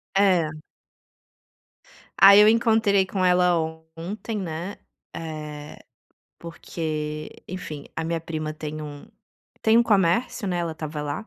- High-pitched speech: No, medium, 170 Hz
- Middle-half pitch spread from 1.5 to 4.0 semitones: No, average, 4.4 semitones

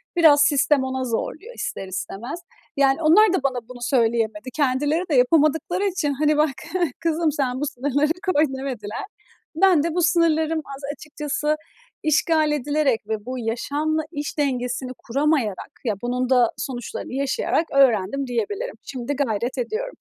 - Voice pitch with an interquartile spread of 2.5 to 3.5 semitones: No, average, 3.9 semitones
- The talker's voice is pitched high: Yes, very high, 280 Hz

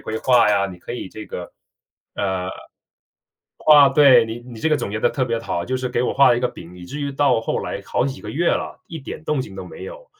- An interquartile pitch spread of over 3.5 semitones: Yes, average, 5.2 semitones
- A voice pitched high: No, low, 125 Hz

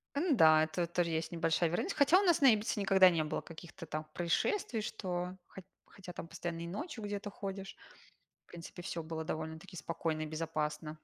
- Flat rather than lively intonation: No, average, 3.8 semitones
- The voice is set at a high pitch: No, medium, 175 Hz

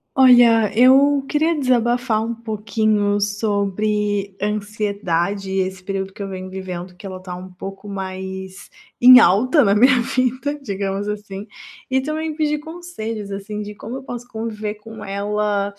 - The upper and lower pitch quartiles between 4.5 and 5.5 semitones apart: No, average, 3.7 semitones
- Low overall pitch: No, high, 210 Hz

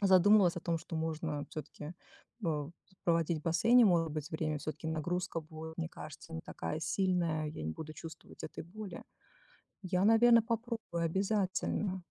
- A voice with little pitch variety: No, average, 3.2 semitones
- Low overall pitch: No, medium, 170 Hz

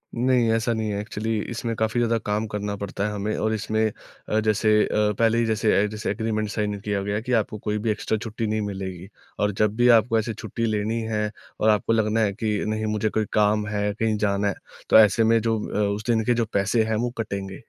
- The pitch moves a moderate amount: No, narrow, 1.4 semitones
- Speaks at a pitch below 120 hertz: Yes, low, 110 Hz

